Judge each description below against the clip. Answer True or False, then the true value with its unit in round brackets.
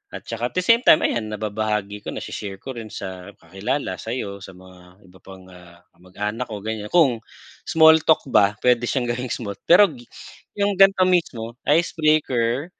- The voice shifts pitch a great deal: True (7.1 semitones)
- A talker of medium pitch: False (115 Hz)